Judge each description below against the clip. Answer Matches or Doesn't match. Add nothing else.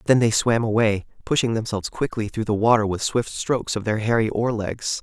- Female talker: Doesn't match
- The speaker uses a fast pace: Matches